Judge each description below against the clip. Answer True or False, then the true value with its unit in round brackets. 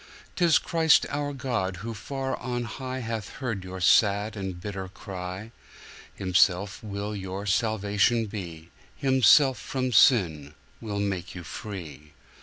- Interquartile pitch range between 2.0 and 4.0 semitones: False (4.6 semitones)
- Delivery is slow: True (115 wpm)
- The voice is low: True (105 Hz)